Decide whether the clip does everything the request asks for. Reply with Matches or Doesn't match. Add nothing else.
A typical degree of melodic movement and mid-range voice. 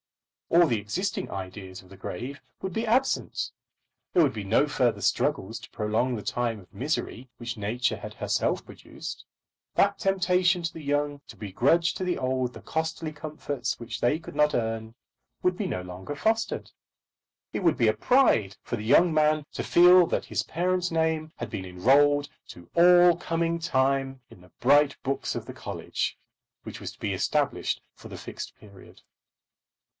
Doesn't match